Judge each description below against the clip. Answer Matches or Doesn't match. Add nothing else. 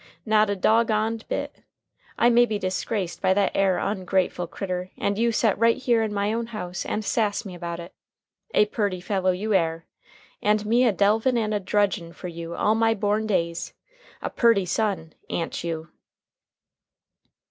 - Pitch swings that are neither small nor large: Matches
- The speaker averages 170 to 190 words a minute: Matches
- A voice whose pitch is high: Matches